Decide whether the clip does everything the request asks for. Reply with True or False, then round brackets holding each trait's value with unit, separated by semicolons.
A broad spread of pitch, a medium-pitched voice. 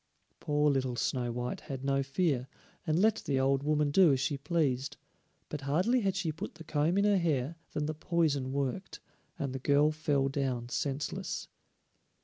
False (3.2 semitones; 145 Hz)